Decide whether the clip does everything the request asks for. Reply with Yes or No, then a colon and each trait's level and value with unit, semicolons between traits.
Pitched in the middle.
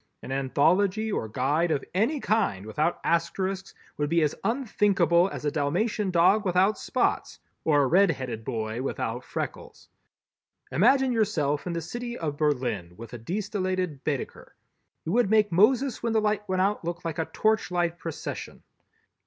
Yes: medium, 175 Hz